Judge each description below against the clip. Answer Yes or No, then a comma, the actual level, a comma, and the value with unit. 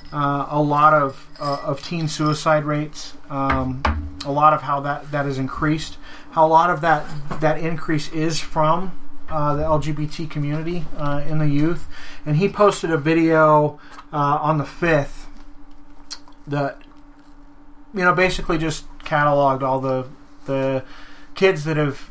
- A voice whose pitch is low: No, medium, 155 Hz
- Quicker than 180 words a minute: No, average, 150 wpm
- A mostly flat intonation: Yes, narrow, 2.2 semitones